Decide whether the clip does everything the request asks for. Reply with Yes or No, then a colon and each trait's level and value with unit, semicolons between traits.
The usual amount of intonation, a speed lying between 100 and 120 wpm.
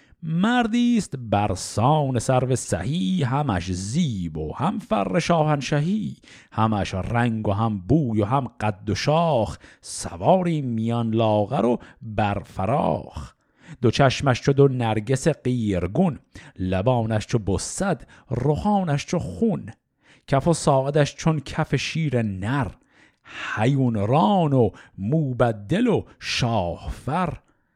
No: wide, 6.3 semitones; average, 110 wpm